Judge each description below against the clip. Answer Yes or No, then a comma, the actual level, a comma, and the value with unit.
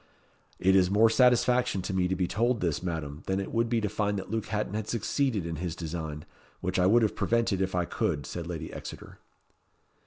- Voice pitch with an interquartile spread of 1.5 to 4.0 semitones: No, average, 4.4 semitones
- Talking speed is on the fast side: Yes, fast, 215 wpm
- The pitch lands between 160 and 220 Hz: No, very low, 95 Hz